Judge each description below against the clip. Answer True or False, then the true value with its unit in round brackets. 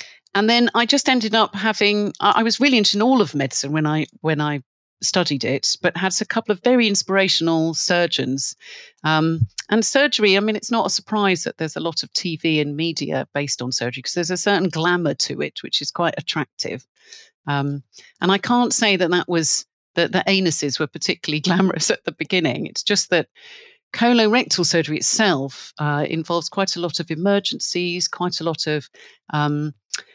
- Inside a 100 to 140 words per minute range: False (190 wpm)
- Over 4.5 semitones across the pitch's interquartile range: True (5.5 semitones)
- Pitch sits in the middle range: True (175 Hz)